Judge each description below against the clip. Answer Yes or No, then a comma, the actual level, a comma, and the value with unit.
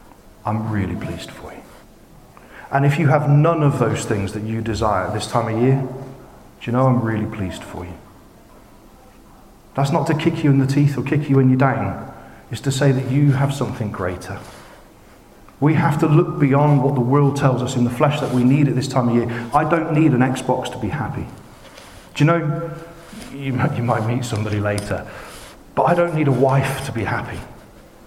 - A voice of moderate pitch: No, low, 130 Hz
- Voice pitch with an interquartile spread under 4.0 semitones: No, average, 4.3 semitones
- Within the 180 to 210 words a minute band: Yes, fast, 205 wpm